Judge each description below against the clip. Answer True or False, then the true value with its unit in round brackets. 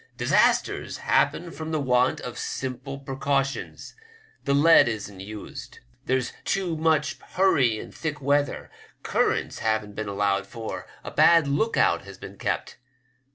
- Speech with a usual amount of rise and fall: False (5.7 semitones)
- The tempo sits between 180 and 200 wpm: False (145 wpm)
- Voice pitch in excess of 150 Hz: False (135 Hz)